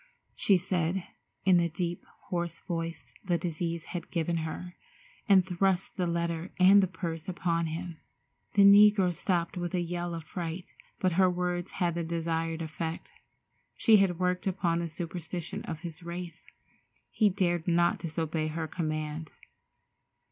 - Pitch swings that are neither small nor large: No, narrow, 1.8 semitones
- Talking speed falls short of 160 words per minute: Yes, average, 150 wpm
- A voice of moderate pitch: Yes, medium, 175 Hz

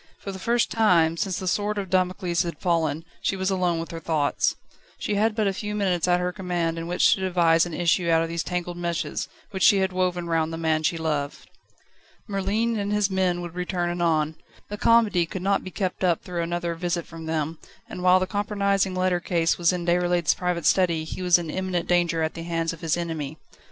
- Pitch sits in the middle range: Yes, medium, 175 Hz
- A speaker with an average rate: No, fast, 220 wpm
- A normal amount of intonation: No, narrow, 2.2 semitones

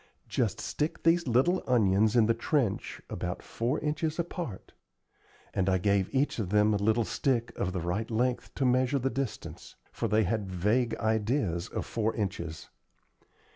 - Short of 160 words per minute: No, average, 165 wpm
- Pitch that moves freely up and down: No, average, 4.5 semitones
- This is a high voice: No, low, 115 Hz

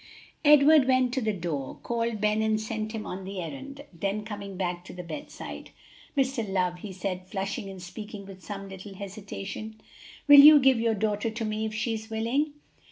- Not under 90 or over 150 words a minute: No, average, 190 wpm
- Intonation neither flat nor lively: Yes, average, 3.2 semitones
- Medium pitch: No, high, 215 Hz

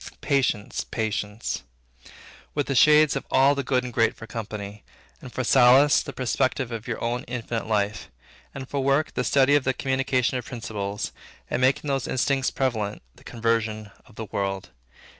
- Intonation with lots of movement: No, average, 3.4 semitones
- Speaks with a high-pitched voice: No, low, 125 Hz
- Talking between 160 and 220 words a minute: Yes, average, 170 wpm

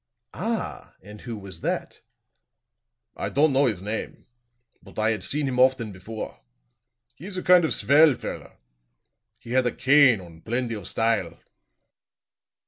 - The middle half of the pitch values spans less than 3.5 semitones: No, average, 4.7 semitones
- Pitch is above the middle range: No, low, 120 Hz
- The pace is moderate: Yes, average, 150 wpm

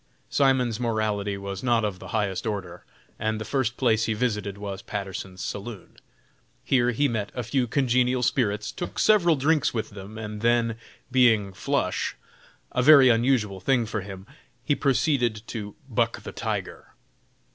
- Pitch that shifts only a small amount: No, average, 3.6 semitones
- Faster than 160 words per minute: No, average, 155 wpm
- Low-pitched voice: Yes, low, 115 Hz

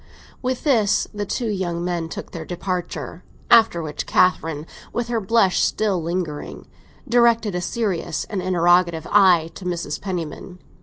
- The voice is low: No, medium, 180 Hz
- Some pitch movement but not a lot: Yes, average, 3.7 semitones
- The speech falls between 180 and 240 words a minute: No, average, 145 wpm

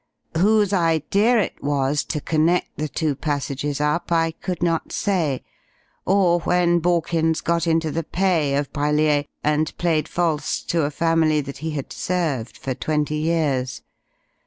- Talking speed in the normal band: Yes, average, 150 wpm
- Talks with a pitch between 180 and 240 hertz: No, medium, 160 Hz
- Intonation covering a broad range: No, average, 2.7 semitones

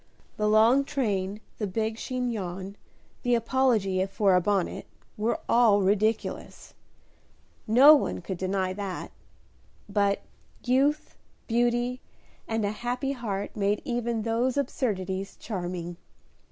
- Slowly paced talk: Yes, slow, 115 wpm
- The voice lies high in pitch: Yes, high, 215 Hz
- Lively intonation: No, average, 3.7 semitones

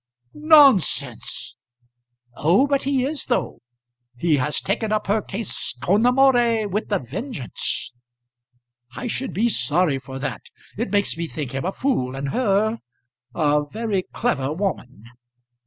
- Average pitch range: No, wide, 8.5 semitones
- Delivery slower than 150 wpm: Yes, average, 140 wpm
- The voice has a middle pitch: No, high, 200 Hz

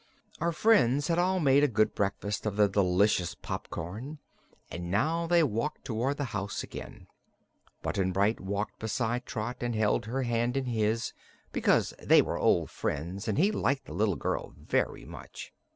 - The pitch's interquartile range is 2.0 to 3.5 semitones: No, wide, 5.4 semitones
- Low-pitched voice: Yes, low, 115 Hz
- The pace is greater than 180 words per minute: No, average, 170 wpm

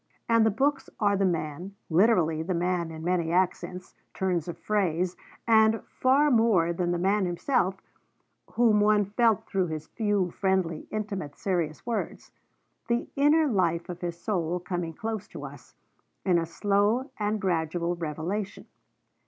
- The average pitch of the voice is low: No, medium, 185 Hz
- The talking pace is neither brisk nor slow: Yes, average, 155 wpm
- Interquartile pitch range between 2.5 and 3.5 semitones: No, average, 3.9 semitones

